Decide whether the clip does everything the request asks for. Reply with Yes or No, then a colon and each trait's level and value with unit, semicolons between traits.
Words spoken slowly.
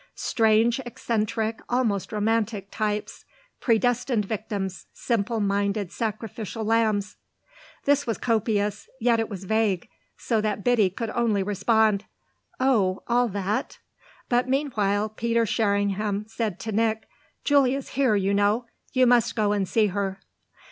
Yes: slow, 125 wpm